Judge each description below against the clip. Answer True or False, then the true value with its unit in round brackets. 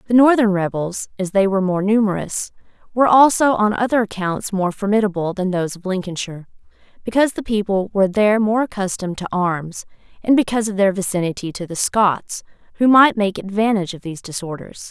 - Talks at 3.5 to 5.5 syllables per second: False (6.1 syllables/s)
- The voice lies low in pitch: False (200 Hz)